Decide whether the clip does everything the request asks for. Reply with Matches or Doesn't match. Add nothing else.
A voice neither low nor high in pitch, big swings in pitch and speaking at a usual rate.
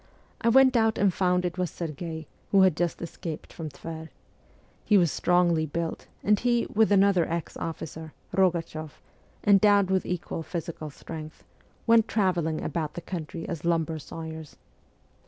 Doesn't match